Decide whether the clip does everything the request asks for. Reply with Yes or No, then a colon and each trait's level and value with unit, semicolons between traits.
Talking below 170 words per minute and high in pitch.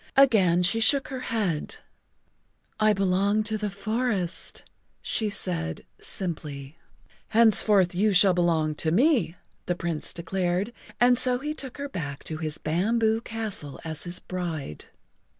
Yes: average, 140 wpm; high, 195 Hz